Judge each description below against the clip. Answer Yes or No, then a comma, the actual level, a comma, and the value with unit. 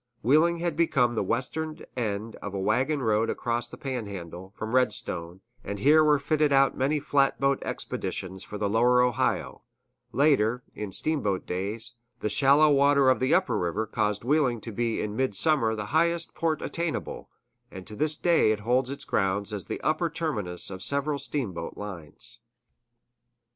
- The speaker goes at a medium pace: Yes, average, 165 wpm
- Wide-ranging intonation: Yes, wide, 5.8 semitones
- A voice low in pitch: Yes, low, 125 Hz